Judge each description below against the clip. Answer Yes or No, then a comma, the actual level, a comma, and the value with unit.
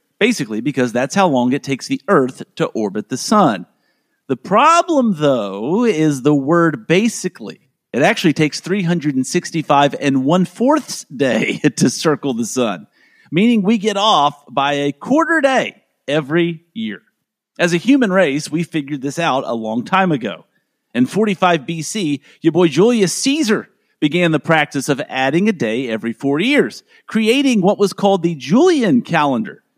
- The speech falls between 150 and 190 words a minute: Yes, average, 155 wpm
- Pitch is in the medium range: Yes, medium, 170 Hz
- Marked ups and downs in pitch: Yes, wide, 7.2 semitones